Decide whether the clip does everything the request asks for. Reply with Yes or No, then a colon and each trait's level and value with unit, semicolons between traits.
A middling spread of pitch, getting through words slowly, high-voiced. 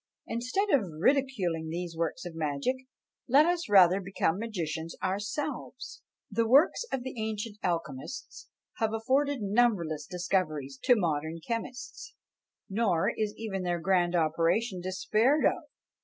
No: wide, 6.0 semitones; slow, 125 wpm; high, 195 Hz